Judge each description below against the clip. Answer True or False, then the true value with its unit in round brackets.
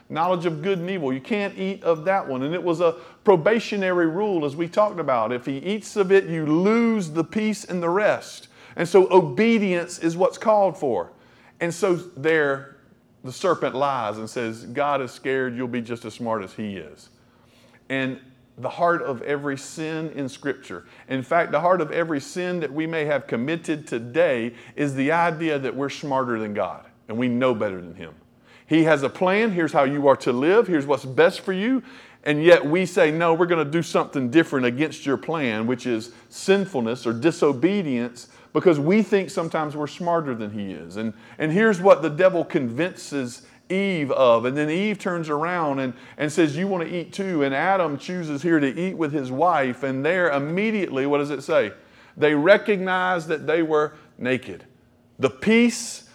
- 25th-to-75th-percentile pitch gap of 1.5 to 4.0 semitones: False (5.5 semitones)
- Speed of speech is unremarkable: True (195 wpm)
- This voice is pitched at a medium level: True (160 Hz)